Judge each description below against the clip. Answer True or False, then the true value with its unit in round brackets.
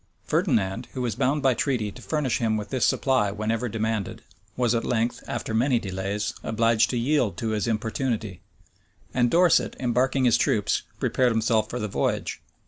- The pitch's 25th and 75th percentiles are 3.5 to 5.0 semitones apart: False (2.8 semitones)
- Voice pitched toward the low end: True (115 Hz)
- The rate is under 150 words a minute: False (170 wpm)